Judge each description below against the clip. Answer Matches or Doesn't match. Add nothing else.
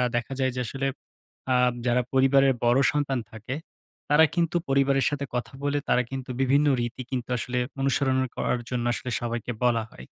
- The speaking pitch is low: Matches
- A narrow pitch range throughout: Matches